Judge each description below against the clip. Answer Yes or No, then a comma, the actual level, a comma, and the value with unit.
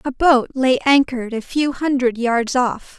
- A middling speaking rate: Yes, average, 180 wpm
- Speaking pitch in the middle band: No, very high, 255 Hz